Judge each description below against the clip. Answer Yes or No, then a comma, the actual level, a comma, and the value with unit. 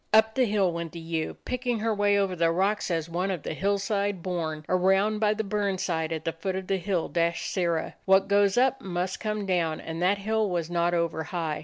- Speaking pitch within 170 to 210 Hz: Yes, medium, 185 Hz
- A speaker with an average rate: No, fast, 225 wpm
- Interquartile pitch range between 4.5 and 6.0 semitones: No, average, 3.3 semitones